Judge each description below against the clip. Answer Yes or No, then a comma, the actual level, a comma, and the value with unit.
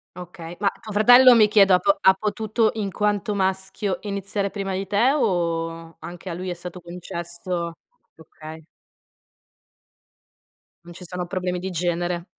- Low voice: No, medium, 185 Hz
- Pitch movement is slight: No, average, 3.0 semitones